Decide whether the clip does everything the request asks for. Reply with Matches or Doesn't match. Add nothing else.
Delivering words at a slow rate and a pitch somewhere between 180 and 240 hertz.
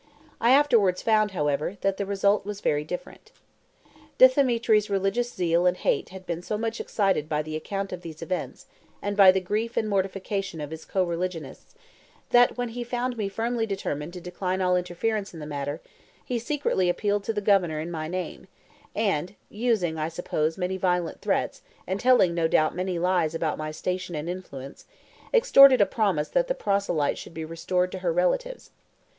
Doesn't match